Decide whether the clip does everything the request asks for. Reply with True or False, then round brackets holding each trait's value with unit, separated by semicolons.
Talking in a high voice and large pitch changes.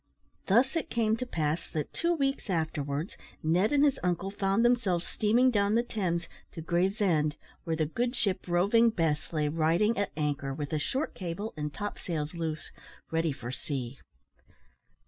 False (175 Hz; 6.0 semitones)